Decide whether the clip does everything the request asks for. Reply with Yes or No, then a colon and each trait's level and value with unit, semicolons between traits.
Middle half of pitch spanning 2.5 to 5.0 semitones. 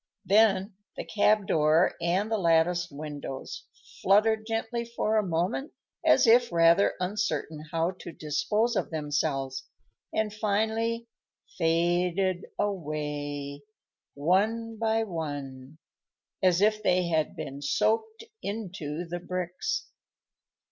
No: wide, 5.6 semitones